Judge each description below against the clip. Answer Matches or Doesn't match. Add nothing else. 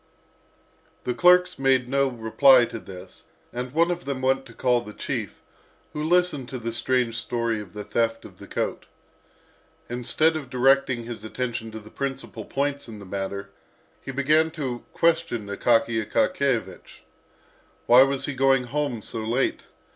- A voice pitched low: Matches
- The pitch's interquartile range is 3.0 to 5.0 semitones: Matches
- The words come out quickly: Doesn't match